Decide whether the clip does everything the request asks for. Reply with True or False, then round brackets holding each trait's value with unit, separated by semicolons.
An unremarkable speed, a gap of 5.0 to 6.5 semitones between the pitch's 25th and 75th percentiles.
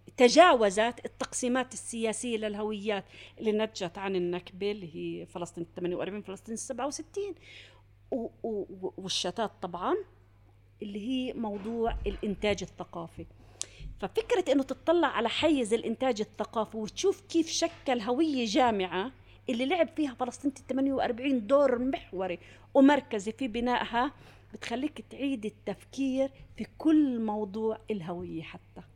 True (110 wpm; 5.3 semitones)